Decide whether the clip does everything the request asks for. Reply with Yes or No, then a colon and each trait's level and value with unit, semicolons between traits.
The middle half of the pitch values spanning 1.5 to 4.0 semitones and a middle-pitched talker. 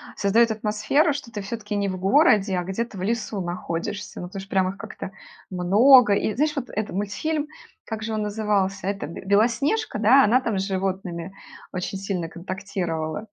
No: average, 3.1 semitones; high, 205 Hz